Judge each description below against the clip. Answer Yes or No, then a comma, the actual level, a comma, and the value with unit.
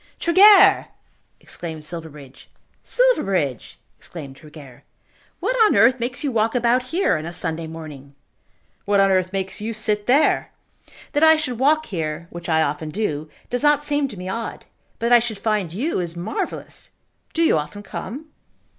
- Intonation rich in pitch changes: Yes, wide, 8.1 semitones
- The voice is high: Yes, high, 205 Hz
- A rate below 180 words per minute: Yes, average, 165 wpm